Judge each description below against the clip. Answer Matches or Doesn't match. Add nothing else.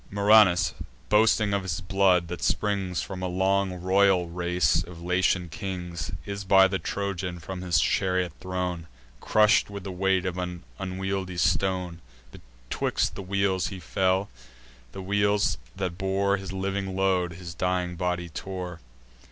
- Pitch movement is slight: Matches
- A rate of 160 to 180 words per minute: Doesn't match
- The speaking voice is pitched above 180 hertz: Doesn't match